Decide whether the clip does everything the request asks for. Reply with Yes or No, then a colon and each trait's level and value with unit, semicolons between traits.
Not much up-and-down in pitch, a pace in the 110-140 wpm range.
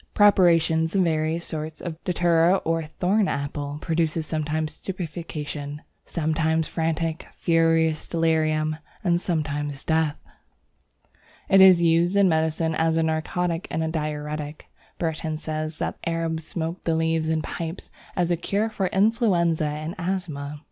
Yes: narrow, 1.7 semitones; slow, 135 wpm